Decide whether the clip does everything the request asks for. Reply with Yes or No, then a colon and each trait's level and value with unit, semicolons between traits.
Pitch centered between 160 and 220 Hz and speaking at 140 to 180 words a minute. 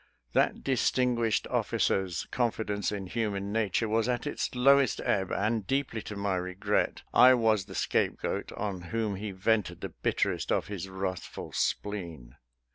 No: low, 105 Hz; average, 150 wpm